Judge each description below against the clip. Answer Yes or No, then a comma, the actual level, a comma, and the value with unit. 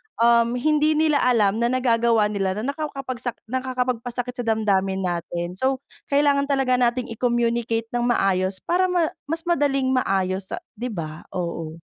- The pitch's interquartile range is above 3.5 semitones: Yes, average, 4.6 semitones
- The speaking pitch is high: Yes, high, 240 Hz